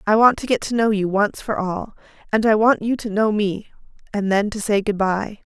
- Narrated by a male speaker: No, female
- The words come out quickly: Yes, fast, 250 wpm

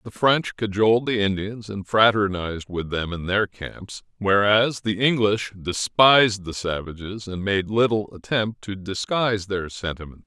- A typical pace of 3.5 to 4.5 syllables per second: Yes, 4.4 syllables/s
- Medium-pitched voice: No, low, 105 Hz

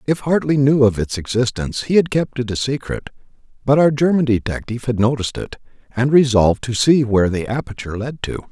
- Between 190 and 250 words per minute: Yes, average, 195 wpm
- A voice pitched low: Yes, low, 125 Hz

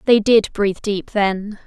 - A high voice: Yes, high, 205 Hz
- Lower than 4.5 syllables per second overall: Yes, 4.1 syllables/s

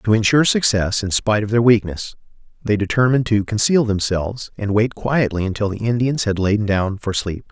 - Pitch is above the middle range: No, low, 105 Hz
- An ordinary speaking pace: Yes, average, 190 wpm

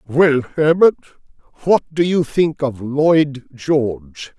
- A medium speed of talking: No, slow, 125 wpm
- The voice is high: No, medium, 140 Hz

